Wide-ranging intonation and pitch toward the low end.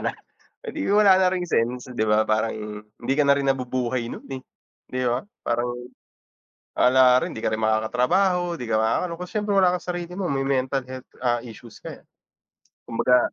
Yes: wide, 6.9 semitones; low, 130 Hz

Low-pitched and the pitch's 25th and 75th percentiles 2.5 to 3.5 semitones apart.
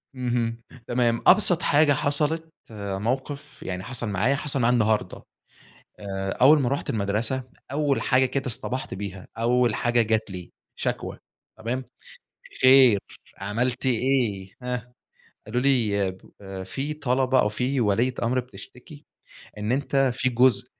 No: low, 125 Hz; average, 3.9 semitones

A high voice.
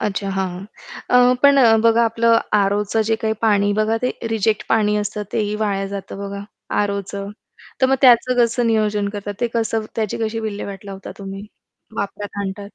Yes: high, 210 Hz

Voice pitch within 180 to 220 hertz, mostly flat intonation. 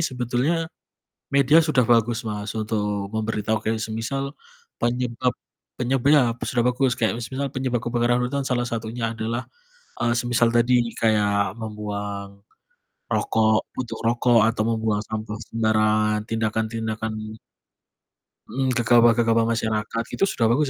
No: low, 115 Hz; narrow, 2.0 semitones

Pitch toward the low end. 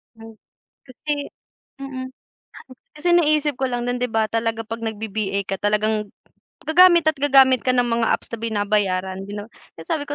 No: high, 230 Hz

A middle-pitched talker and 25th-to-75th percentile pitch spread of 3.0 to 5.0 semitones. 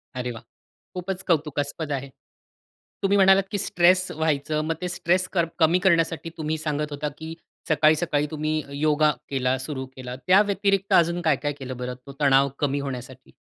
Yes: medium, 155 Hz; average, 3.8 semitones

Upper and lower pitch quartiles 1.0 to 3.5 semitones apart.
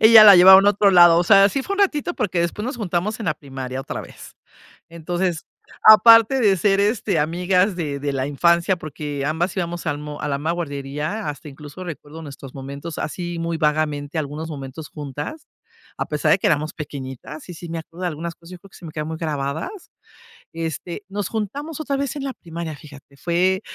No: average, 4.7 semitones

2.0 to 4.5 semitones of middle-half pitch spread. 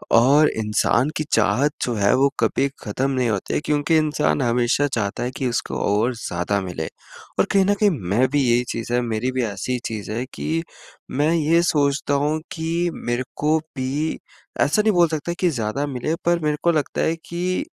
No: average, 5.1 semitones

